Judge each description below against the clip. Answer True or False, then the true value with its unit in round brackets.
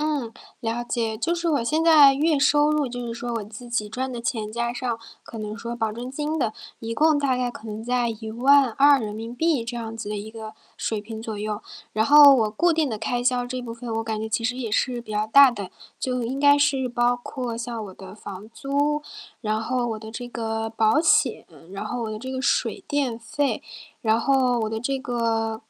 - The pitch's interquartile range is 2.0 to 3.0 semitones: False (3.5 semitones)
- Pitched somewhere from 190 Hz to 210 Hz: False (240 Hz)